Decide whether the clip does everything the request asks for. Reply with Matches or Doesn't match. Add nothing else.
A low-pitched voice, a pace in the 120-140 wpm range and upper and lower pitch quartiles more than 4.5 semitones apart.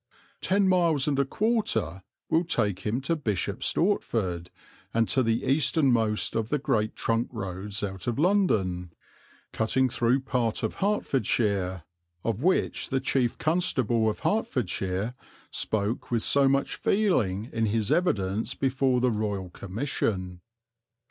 Matches